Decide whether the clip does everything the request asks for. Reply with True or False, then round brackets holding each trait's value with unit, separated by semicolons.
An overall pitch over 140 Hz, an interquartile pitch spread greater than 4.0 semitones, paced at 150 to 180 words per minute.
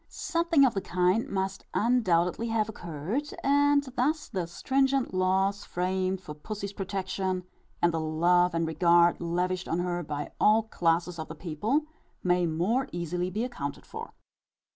True (185 Hz; 4.5 semitones; 155 wpm)